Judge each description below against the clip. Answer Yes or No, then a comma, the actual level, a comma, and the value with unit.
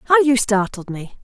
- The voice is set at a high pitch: Yes, high, 220 Hz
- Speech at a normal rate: Yes, average, 195 wpm